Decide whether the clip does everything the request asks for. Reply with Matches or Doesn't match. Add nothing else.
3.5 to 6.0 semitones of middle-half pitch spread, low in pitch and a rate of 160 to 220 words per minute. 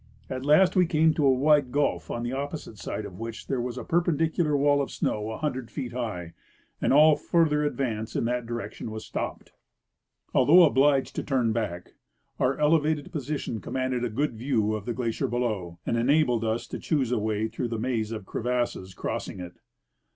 Matches